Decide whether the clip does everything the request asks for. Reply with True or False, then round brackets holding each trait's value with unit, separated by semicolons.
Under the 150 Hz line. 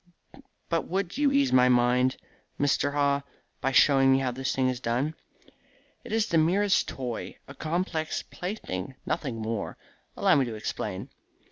True (135 Hz)